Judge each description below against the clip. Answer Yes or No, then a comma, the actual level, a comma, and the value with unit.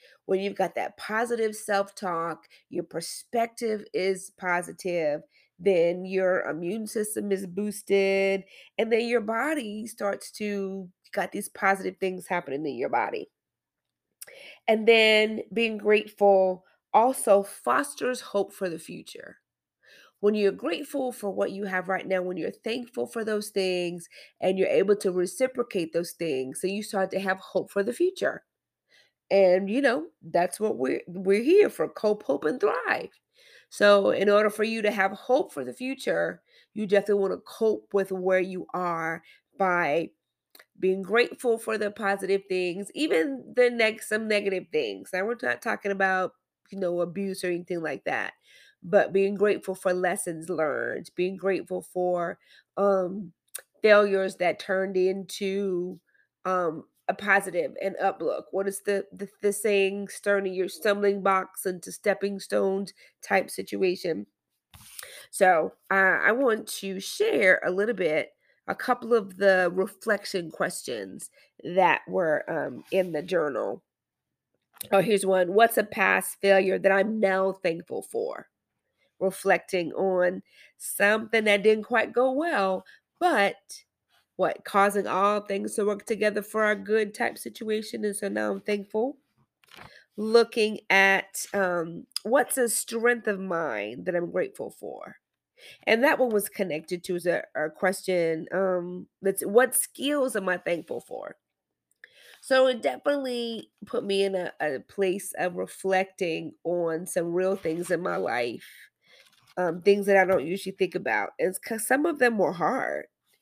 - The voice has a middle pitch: No, high, 195 Hz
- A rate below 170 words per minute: Yes, average, 150 wpm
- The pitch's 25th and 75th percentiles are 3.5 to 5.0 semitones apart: No, average, 2.8 semitones